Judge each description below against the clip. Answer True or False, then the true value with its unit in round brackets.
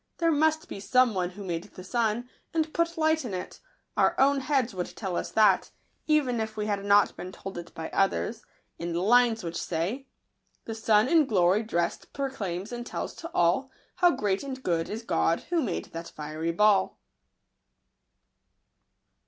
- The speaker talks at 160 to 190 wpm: True (180 wpm)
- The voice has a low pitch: False (215 Hz)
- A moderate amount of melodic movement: False (6.5 semitones)